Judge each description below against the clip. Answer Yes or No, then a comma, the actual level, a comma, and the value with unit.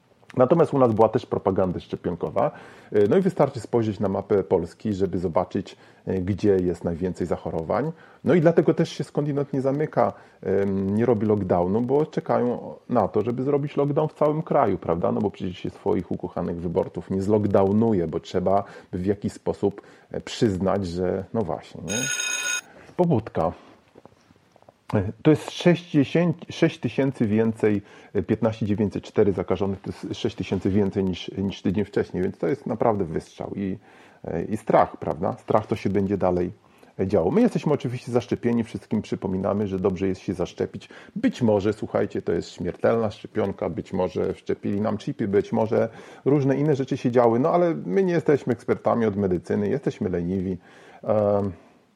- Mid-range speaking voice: No, low, 110 Hz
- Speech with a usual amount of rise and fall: No, wide, 6.5 semitones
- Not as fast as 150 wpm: No, average, 155 wpm